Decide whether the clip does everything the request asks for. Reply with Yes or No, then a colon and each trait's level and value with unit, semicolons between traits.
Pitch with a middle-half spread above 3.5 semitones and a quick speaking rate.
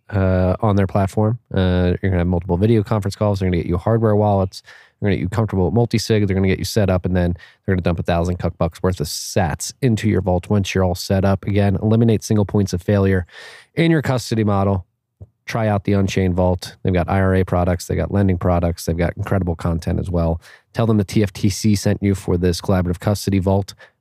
No: average, 2.7 semitones; fast, 225 wpm